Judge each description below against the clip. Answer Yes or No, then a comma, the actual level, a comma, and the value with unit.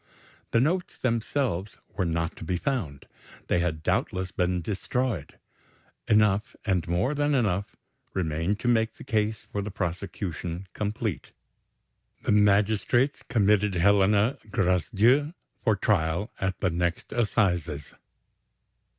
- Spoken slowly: Yes, slow, 120 wpm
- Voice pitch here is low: Yes, low, 100 Hz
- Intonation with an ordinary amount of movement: Yes, average, 4.0 semitones